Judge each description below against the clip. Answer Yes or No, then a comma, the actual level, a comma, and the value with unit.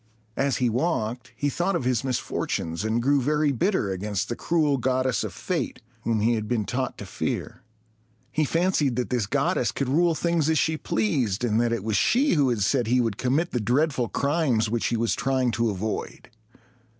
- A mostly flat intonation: No, average, 4.5 semitones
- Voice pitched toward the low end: Yes, low, 125 Hz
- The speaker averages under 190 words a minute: No, average, 200 wpm